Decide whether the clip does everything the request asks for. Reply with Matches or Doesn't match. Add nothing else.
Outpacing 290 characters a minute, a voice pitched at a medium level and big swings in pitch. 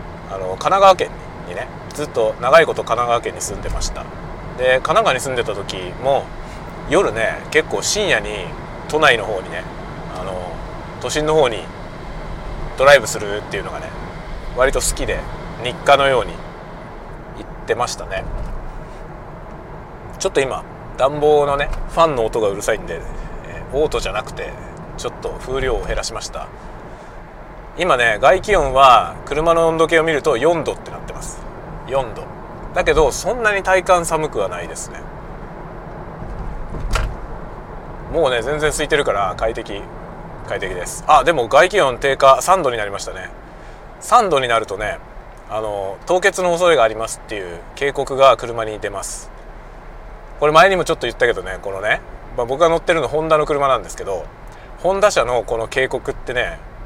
Matches